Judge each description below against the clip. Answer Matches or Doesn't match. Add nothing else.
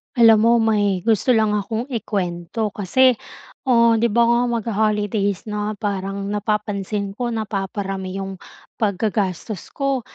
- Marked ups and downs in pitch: Doesn't match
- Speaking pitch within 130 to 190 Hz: Doesn't match